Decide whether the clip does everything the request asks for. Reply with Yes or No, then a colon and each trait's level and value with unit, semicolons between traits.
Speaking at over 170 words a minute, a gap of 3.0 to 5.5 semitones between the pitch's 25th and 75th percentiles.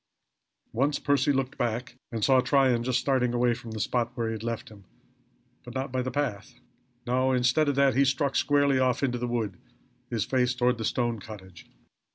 No: average, 195 wpm; narrow, 2.4 semitones